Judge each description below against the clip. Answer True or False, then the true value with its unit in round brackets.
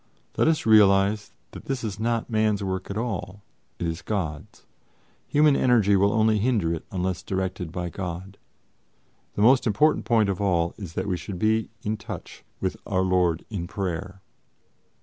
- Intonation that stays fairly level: False (3.1 semitones)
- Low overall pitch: True (100 Hz)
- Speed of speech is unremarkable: True (170 wpm)